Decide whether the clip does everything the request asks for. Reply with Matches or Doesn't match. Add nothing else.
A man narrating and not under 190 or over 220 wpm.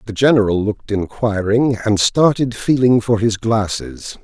Doesn't match